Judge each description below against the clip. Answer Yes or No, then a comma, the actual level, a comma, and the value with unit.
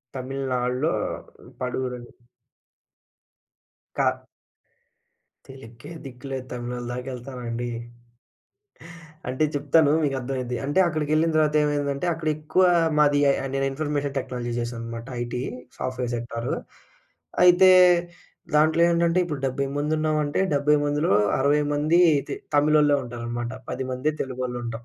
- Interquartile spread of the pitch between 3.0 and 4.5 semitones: Yes, average, 3.3 semitones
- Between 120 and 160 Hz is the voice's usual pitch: Yes, low, 135 Hz